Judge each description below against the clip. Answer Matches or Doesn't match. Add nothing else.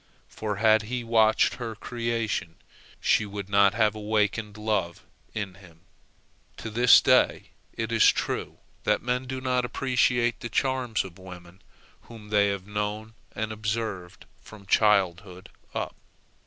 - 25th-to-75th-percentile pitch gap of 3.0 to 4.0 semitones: Doesn't match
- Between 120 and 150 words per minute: Matches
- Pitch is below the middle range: Matches